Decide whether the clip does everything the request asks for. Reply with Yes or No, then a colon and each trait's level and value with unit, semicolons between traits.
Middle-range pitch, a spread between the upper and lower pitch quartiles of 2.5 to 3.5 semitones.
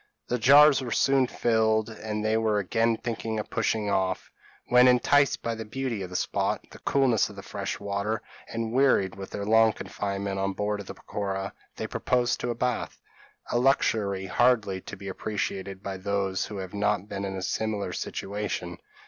No: low, 105 Hz; average, 2.9 semitones